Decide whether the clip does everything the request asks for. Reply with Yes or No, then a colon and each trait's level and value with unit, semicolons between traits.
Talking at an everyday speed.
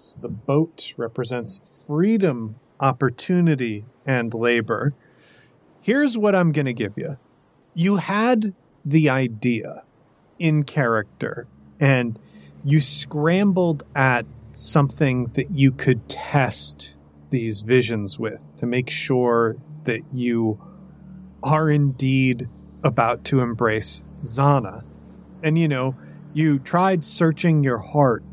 No: slow, 110 wpm